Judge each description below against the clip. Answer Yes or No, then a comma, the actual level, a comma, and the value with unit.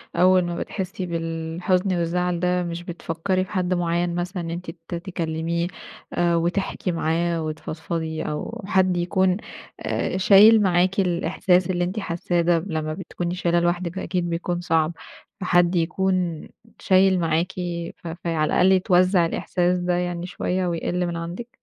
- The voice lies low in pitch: No, medium, 175 Hz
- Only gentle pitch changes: Yes, narrow, 1.6 semitones